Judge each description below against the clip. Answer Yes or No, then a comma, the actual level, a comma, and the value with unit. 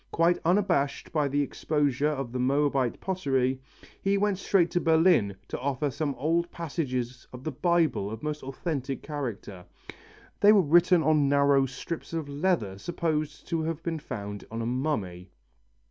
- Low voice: No, medium, 145 Hz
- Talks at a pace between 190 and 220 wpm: No, average, 160 wpm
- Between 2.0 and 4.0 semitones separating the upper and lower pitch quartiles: No, average, 4.4 semitones